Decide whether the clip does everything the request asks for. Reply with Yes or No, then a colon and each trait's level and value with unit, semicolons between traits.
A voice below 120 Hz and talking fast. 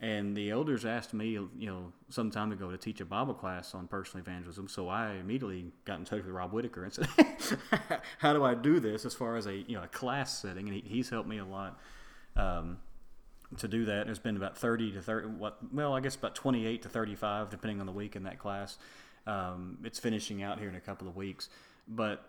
Yes: low, 105 Hz; fast, 230 wpm